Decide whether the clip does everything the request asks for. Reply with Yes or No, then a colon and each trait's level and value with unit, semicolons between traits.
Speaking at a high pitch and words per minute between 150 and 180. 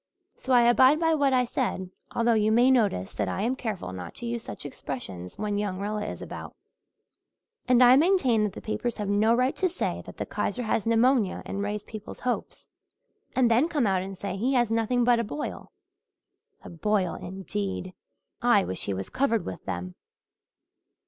No: high, 220 Hz; average, 190 wpm